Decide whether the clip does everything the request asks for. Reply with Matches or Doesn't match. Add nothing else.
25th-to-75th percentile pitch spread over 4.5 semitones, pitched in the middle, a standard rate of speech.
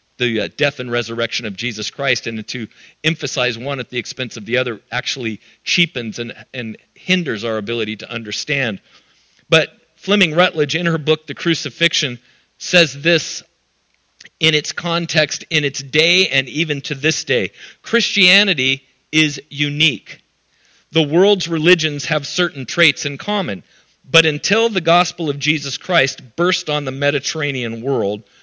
Matches